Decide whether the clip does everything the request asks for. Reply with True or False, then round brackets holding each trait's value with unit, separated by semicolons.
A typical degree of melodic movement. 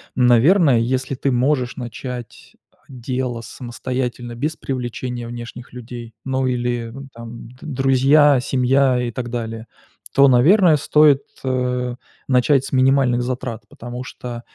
False (1.8 semitones)